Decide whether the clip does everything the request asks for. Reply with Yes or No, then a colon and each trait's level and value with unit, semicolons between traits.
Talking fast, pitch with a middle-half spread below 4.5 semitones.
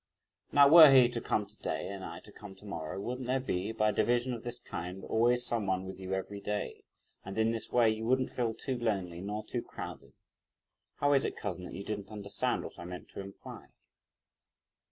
Yes: fast, 215 wpm; average, 4.0 semitones